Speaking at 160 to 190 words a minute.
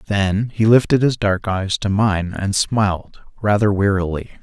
Yes: average, 165 wpm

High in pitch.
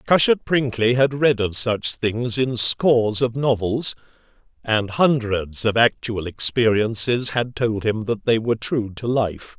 No: low, 115 Hz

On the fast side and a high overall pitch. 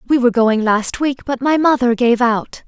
Yes: fast, 225 wpm; high, 245 Hz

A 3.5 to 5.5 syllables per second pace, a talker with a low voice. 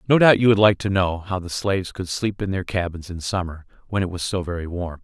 No: 5.9 syllables/s; very low, 95 Hz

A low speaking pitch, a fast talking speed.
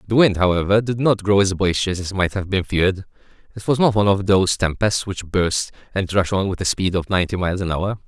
Yes: very low, 95 Hz; fast, 245 wpm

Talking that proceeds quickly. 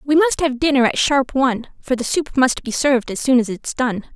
Yes: fast, 260 wpm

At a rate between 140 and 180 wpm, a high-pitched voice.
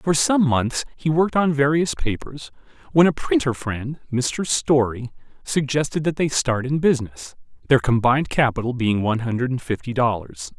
No: average, 165 wpm; low, 135 Hz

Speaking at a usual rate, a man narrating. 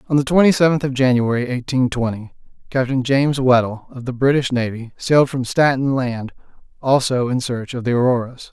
Yes: average, 175 wpm; male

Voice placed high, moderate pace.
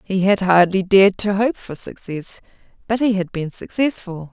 Yes: high, 195 Hz; average, 180 wpm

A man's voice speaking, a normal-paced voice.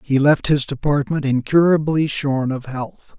Yes: male; average, 150 wpm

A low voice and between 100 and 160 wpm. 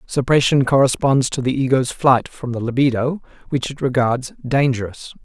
Yes: low, 130 Hz; average, 150 wpm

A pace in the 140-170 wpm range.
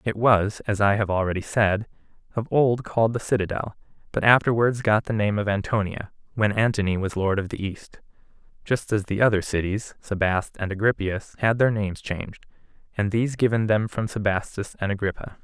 No: average, 180 wpm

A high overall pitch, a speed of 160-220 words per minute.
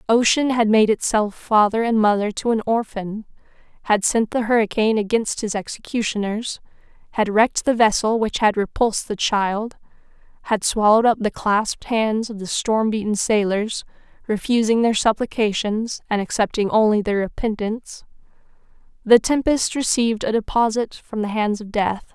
No: high, 220 Hz; average, 150 wpm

